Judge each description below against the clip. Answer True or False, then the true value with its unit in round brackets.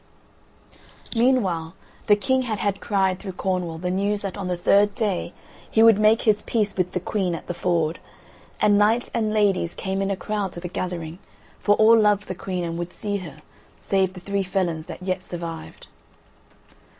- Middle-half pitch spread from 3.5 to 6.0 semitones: False (2.8 semitones)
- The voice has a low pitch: False (190 Hz)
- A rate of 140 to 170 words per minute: False (185 wpm)